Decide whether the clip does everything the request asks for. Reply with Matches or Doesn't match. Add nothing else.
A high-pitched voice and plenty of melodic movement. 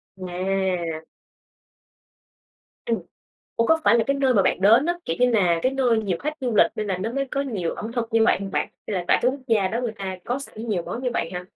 Doesn't match